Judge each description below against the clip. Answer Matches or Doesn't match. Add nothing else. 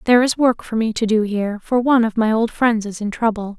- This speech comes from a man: Doesn't match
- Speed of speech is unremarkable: Doesn't match